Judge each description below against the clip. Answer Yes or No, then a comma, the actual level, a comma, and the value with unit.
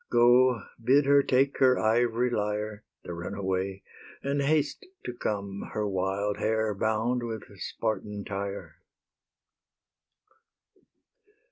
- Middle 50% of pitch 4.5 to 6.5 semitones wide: No, average, 3.7 semitones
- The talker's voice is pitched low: Yes, low, 110 Hz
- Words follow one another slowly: Yes, slow, 105 wpm